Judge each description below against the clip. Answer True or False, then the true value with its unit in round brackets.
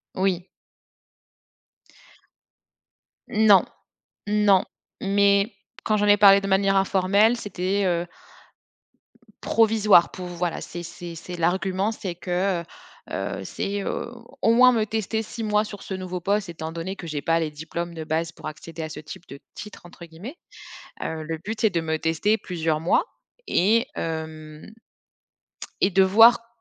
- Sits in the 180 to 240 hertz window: True (185 Hz)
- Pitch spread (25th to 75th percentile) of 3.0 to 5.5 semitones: True (3.8 semitones)